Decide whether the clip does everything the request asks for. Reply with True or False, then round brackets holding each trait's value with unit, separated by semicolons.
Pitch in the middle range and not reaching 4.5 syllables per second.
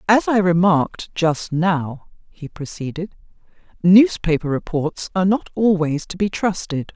True (180 Hz; 4.3 syllables/s)